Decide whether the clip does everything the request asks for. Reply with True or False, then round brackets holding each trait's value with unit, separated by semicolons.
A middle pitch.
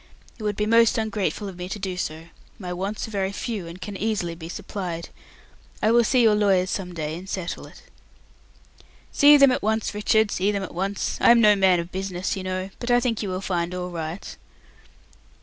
False (195 Hz)